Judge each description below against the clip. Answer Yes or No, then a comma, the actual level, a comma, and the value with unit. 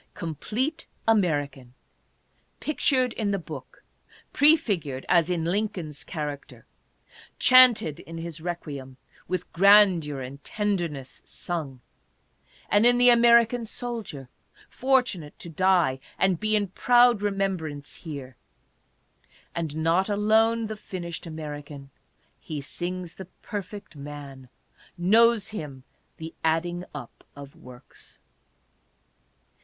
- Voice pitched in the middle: Yes, medium, 175 Hz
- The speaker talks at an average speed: No, slow, 110 wpm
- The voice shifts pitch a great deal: Yes, wide, 6.4 semitones